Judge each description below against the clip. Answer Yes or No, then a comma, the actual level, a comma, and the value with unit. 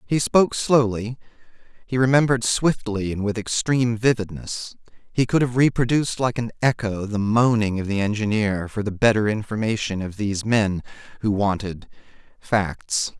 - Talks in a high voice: No, low, 110 Hz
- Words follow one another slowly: No, average, 145 wpm